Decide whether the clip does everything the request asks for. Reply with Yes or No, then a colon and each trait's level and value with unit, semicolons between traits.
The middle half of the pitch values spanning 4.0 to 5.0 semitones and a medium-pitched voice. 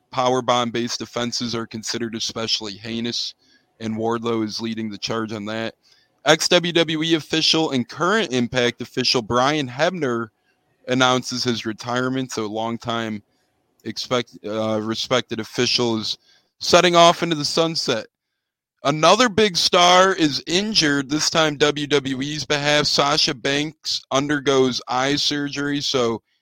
No: average, 4.6 semitones; low, 125 Hz